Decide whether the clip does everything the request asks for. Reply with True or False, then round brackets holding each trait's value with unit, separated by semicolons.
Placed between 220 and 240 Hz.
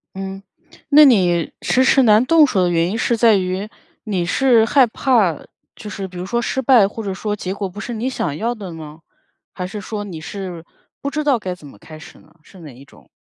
False (200 Hz)